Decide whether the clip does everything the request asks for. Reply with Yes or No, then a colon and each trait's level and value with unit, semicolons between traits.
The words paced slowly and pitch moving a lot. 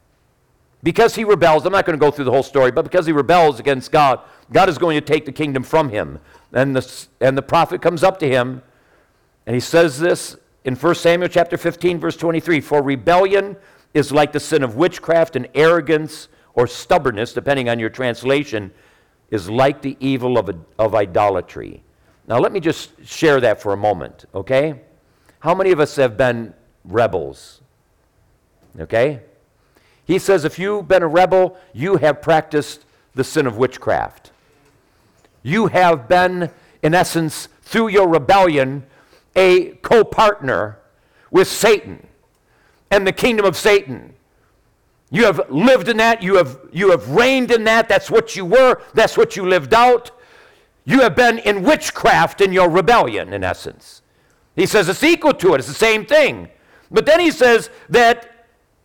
No: average, 170 wpm; wide, 6.5 semitones